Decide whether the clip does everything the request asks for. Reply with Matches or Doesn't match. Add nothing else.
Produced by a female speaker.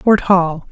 Matches